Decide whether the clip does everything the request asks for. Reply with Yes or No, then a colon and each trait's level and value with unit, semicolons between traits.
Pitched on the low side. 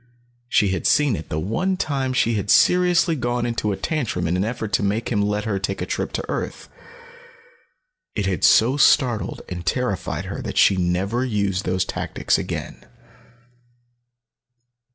Yes: low, 105 Hz